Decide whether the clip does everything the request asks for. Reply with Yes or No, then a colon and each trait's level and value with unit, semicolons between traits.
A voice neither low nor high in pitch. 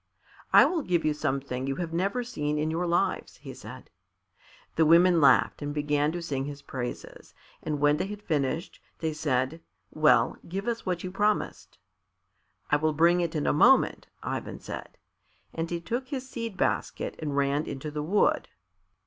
Yes: medium, 160 Hz